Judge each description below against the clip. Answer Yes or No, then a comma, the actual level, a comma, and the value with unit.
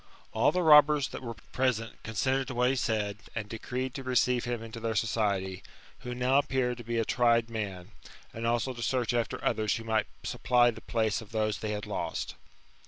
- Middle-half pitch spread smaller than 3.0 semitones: Yes, narrow, 2.4 semitones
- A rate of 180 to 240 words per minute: Yes, average, 200 wpm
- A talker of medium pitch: No, low, 115 Hz